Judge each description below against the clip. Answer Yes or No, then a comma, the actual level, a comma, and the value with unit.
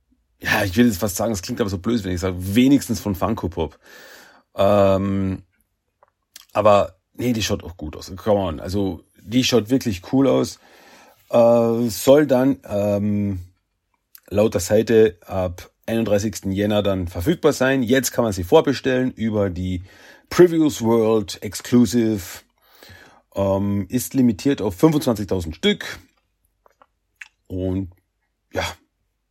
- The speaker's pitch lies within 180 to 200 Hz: No, low, 105 Hz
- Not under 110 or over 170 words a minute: Yes, average, 130 wpm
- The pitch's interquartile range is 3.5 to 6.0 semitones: Yes, average, 3.9 semitones